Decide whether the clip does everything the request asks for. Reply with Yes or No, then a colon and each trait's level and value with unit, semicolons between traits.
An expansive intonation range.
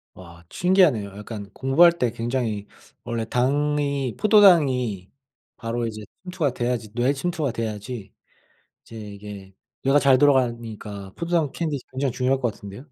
No: average, 4.9 semitones